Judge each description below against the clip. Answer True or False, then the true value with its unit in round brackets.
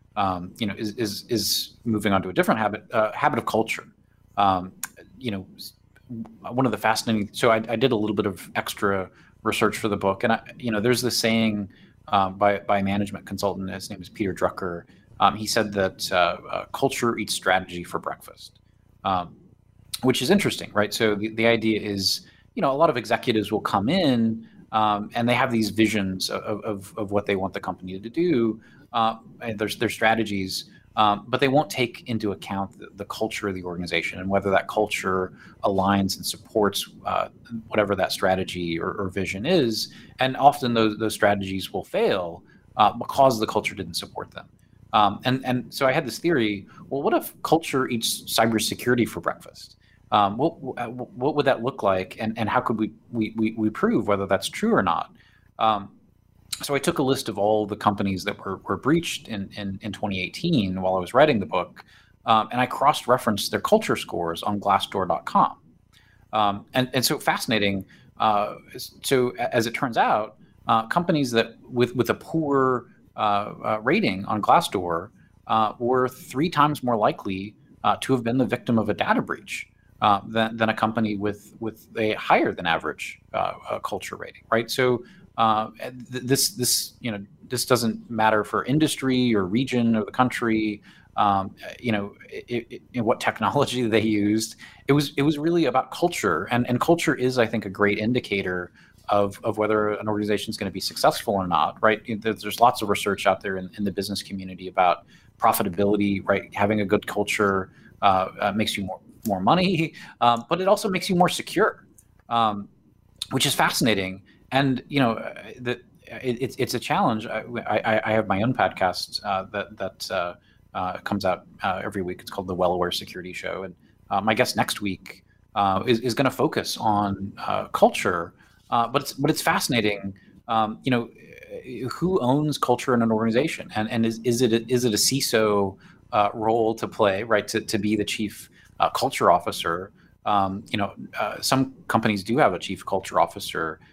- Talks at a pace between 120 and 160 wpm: False (190 wpm)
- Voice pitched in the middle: False (110 Hz)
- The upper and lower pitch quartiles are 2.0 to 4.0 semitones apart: True (3.4 semitones)